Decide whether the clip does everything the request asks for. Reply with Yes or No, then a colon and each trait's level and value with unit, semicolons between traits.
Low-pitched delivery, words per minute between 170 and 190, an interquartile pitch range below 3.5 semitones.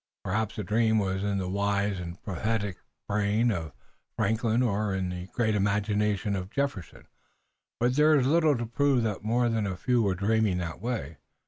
Yes: low, 105 Hz; average, 180 wpm; average, 3.1 semitones